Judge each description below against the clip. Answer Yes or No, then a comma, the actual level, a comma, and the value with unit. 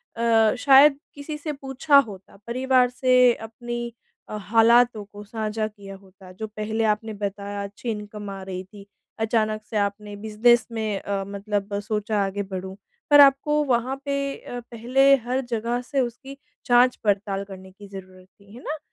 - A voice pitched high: Yes, high, 220 Hz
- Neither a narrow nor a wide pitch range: Yes, average, 3.4 semitones